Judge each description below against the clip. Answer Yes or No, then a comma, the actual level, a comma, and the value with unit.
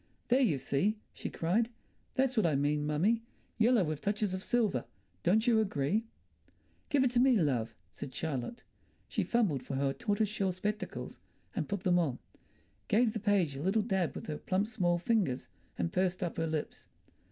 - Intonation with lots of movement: Yes, wide, 6.5 semitones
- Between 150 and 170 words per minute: No, average, 180 wpm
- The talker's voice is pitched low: No, high, 190 Hz